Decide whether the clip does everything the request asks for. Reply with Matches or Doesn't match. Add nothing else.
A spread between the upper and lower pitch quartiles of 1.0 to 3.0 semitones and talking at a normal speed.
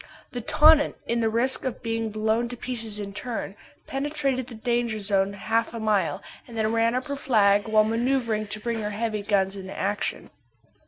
Matches